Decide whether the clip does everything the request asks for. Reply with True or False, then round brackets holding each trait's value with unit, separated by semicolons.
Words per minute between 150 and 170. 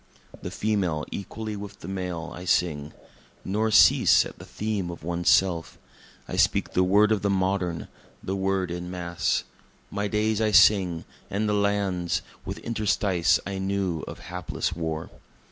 True (160 wpm)